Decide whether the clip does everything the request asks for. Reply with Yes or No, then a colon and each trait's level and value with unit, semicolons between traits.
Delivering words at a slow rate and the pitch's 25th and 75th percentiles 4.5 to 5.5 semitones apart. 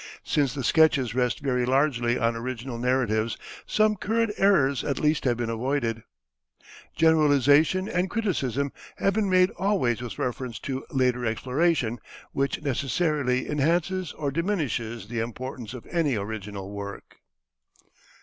Yes: slow, 130 wpm; average, 5.1 semitones